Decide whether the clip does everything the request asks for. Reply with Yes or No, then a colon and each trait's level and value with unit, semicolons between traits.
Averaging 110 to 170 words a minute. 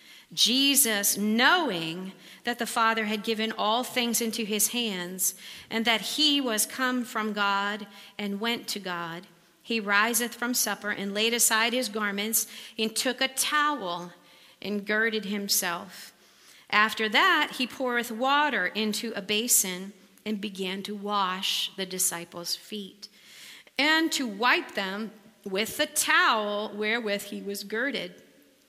Yes: slow, 135 wpm